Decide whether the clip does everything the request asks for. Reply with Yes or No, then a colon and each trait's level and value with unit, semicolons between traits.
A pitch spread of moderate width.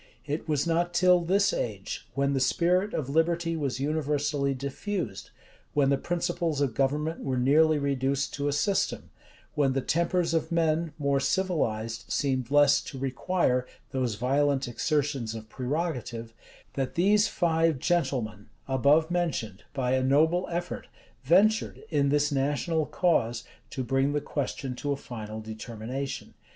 Yes: average, 4.2 semitones